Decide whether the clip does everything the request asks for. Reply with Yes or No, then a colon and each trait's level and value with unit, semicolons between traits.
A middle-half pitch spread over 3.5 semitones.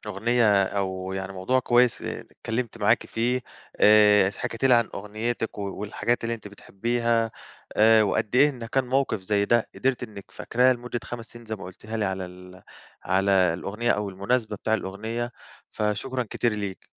No: average, 3.1 semitones